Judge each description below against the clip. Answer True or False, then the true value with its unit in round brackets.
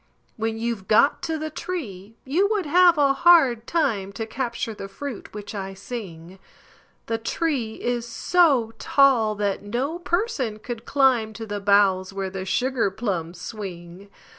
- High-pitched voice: True (225 Hz)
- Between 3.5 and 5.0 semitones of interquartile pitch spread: False (5.6 semitones)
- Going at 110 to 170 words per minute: True (155 wpm)